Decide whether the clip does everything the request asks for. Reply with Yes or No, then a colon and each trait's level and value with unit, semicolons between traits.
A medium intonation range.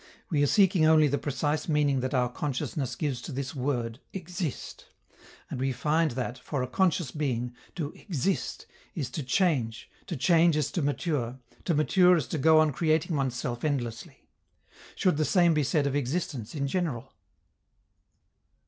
Yes: average, 4.0 semitones